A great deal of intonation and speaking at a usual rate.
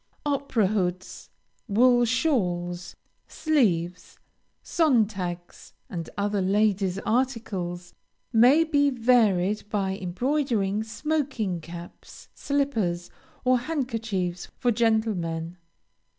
No: wide, 5.9 semitones; slow, 80 wpm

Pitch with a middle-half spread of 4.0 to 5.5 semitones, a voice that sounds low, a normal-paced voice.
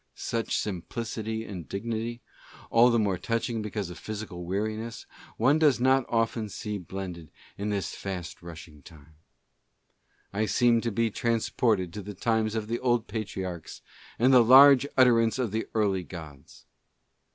No: average, 3.6 semitones; low, 110 Hz; average, 160 wpm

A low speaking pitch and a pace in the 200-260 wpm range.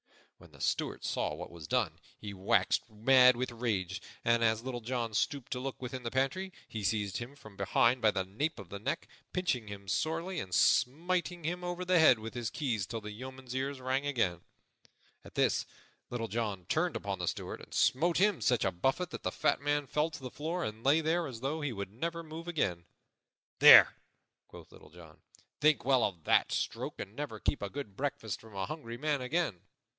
Yes: low, 125 Hz; fast, 205 wpm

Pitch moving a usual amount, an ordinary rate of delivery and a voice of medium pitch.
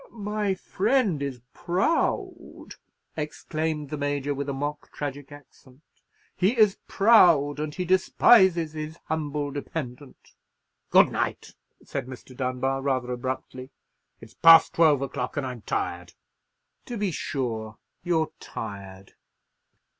No: average, 4.5 semitones; slow, 120 wpm; medium, 145 Hz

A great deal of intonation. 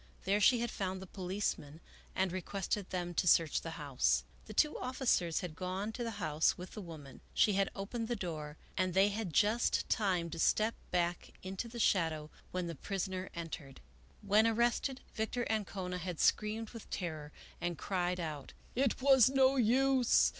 No: average, 4.5 semitones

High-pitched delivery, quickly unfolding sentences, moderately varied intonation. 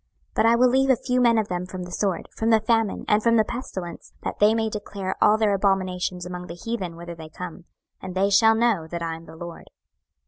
Yes: high, 195 Hz; fast, 245 wpm; average, 3.9 semitones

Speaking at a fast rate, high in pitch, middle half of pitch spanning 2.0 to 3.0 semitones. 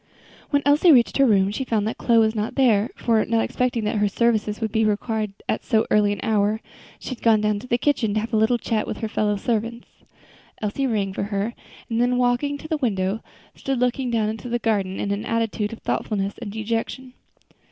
Yes: fast, 220 wpm; high, 225 Hz; narrow, 2.5 semitones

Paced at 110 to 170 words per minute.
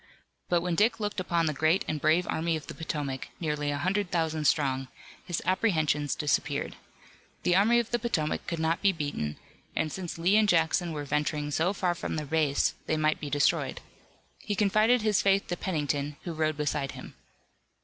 No: average, 190 wpm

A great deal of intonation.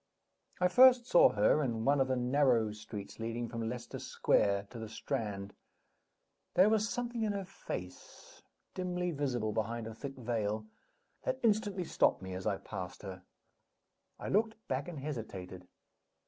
Yes: wide, 8.8 semitones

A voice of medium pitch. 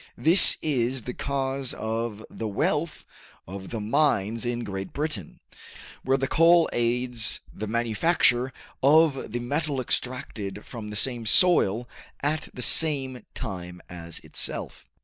No: low, 120 Hz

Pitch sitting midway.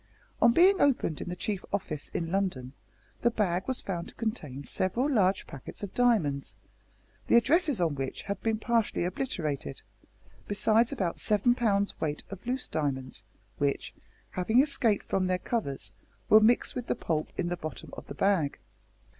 No: high, 195 Hz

